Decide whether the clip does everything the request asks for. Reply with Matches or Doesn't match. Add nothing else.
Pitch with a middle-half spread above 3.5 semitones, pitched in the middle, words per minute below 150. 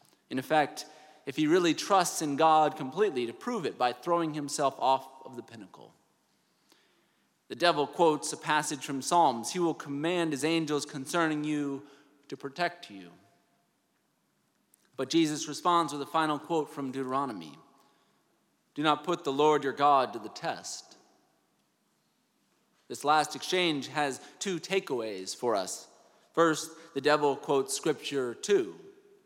Doesn't match